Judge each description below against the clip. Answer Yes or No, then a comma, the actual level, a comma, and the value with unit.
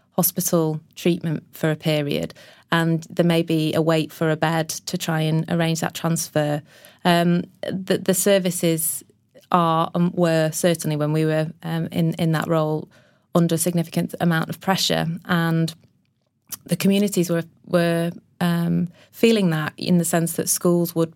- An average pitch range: No, narrow, 1.7 semitones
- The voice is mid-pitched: Yes, medium, 165 Hz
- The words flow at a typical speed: Yes, average, 160 wpm